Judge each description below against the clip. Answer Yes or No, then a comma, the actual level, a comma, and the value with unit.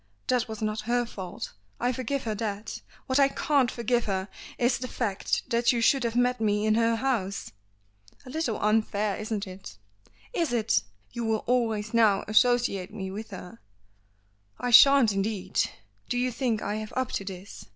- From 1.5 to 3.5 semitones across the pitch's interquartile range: Yes, average, 2.9 semitones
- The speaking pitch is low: No, high, 225 Hz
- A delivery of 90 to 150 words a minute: No, average, 175 wpm